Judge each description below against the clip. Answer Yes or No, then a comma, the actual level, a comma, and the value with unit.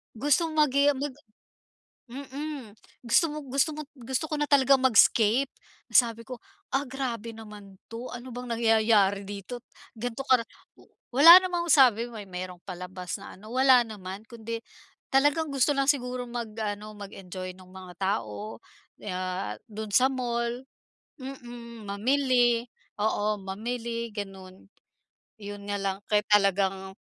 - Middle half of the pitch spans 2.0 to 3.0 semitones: No, average, 4.6 semitones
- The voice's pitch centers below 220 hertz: No, high, 230 Hz